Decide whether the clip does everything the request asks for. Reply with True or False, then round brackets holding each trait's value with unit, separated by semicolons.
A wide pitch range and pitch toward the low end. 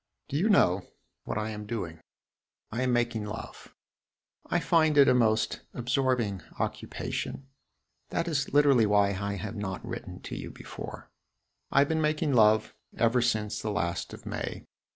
False (5.0 semitones; 115 Hz)